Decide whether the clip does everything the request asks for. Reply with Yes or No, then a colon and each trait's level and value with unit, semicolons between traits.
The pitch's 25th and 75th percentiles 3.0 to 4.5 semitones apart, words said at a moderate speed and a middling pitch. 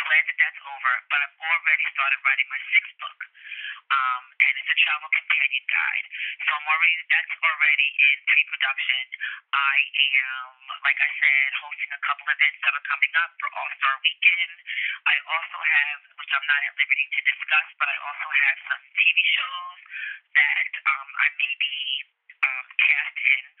Yes: average, 3.6 semitones; average, 180 wpm; medium, 155 Hz